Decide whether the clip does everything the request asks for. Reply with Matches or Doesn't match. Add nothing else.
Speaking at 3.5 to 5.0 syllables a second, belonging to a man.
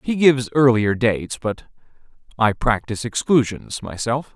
Matches